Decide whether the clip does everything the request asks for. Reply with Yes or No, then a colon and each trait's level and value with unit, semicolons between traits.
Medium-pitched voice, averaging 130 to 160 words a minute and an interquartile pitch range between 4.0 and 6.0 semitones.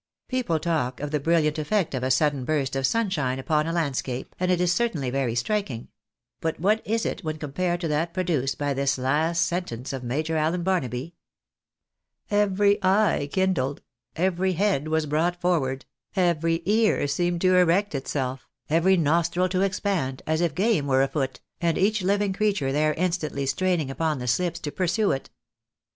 No: medium, 165 Hz; average, 170 wpm; average, 4.8 semitones